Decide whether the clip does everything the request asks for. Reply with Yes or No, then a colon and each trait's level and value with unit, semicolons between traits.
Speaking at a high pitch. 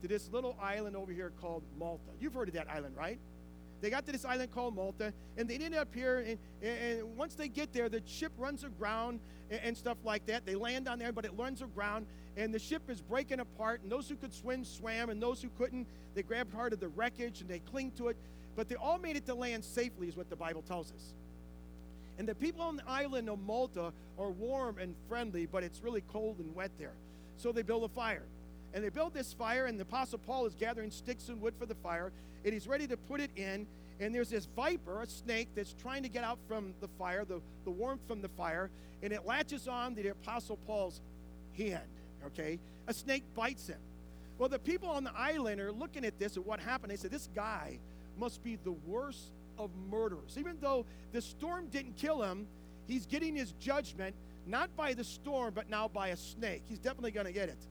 Yes: high, 225 Hz